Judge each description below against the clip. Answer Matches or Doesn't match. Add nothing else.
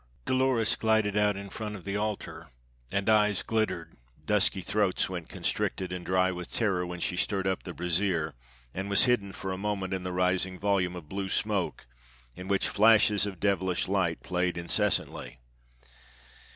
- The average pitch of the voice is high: Doesn't match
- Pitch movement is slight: Matches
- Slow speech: Doesn't match